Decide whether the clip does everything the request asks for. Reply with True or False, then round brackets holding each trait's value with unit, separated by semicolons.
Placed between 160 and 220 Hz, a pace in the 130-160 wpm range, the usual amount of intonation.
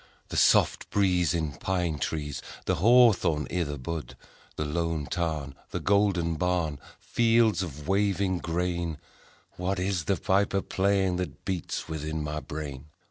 False (85 Hz; 145 wpm; 3.8 semitones)